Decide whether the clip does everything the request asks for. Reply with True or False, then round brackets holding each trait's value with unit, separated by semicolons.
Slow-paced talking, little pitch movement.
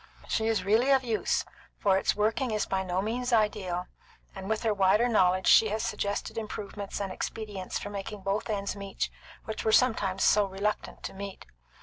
False (185 wpm; 2.2 semitones)